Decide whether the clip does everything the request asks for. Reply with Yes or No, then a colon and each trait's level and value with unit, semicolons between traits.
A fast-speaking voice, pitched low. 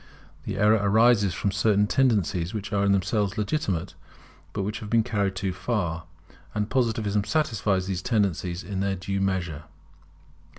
No: average, 155 wpm; low, 100 Hz